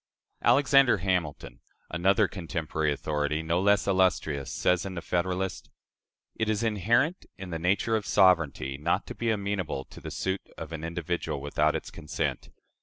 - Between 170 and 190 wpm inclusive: No, average, 160 wpm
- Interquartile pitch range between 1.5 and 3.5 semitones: No, average, 4.2 semitones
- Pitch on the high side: No, very low, 90 Hz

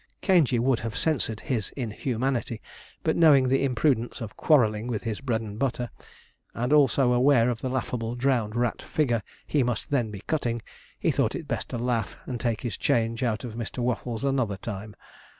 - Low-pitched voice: Yes, low, 120 Hz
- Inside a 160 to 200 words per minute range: Yes, average, 185 wpm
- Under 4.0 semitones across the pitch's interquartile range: Yes, average, 2.7 semitones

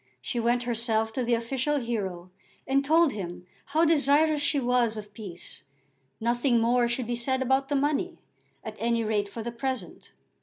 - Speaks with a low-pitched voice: No, high, 240 Hz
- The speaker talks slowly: No, average, 175 wpm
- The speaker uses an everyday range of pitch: Yes, average, 3.5 semitones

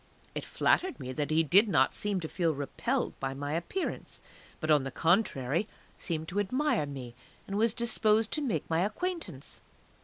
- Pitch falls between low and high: Yes, medium, 175 Hz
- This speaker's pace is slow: No, average, 175 wpm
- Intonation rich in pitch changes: Yes, wide, 7.3 semitones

